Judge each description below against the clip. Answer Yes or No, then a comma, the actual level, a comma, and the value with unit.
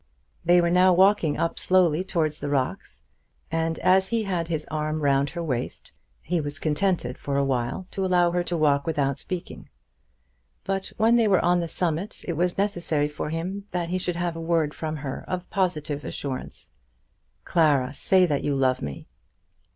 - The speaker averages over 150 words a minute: Yes, average, 180 wpm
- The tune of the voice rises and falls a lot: No, average, 3.7 semitones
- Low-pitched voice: No, medium, 165 Hz